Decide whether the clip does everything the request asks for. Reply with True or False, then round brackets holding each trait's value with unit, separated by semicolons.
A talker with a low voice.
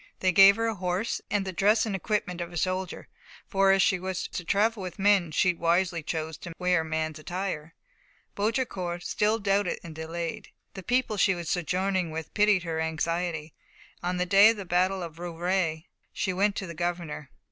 False (180 Hz)